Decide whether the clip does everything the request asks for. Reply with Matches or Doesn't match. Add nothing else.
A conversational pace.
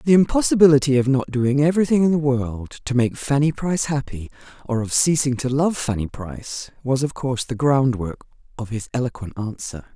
Matches